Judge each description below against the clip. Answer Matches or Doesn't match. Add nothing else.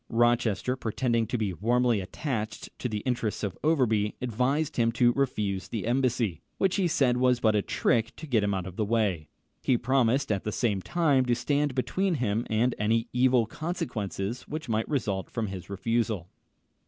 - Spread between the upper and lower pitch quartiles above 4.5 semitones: Doesn't match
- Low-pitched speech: Matches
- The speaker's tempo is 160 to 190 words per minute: Matches